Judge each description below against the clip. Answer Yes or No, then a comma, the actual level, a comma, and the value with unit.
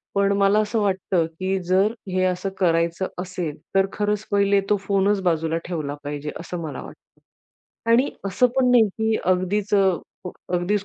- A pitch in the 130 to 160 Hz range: No, high, 190 Hz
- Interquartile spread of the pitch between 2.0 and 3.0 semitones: Yes, average, 2.7 semitones